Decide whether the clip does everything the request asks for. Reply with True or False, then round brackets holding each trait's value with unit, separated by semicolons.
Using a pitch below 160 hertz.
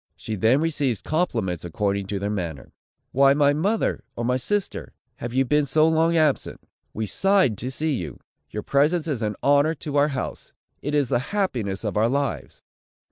True (135 Hz)